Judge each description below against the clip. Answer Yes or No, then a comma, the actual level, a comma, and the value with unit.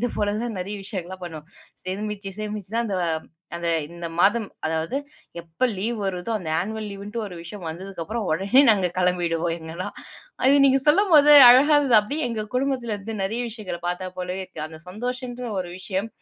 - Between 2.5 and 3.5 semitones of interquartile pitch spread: No, average, 4.7 semitones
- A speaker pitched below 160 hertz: No, high, 205 Hz